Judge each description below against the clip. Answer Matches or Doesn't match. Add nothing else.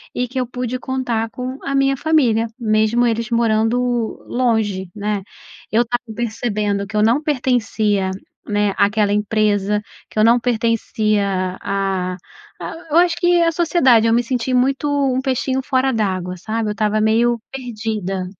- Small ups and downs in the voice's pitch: Doesn't match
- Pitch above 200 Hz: Matches